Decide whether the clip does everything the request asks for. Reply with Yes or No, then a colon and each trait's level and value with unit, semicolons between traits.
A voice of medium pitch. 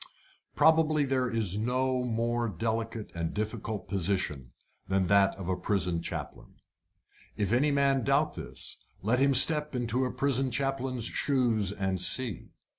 No: low, 115 Hz